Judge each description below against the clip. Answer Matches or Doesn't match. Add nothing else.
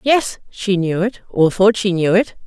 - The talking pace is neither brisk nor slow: Doesn't match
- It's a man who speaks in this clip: Doesn't match